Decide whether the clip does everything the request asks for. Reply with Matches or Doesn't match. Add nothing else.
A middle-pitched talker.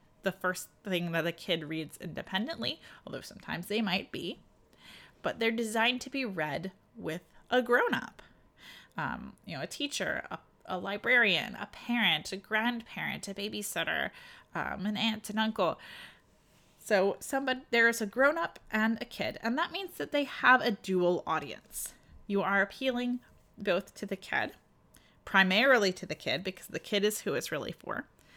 Doesn't match